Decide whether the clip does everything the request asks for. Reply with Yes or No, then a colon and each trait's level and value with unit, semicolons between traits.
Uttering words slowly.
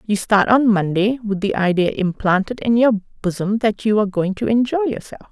No: fast, 205 wpm